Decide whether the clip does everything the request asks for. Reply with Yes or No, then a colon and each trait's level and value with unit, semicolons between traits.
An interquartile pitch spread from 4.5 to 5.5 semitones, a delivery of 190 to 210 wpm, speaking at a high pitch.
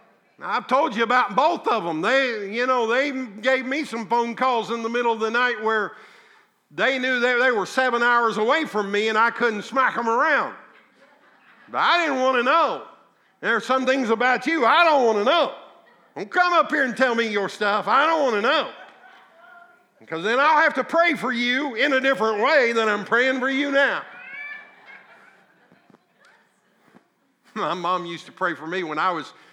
No: average, 3.2 semitones; average, 195 wpm; very high, 250 Hz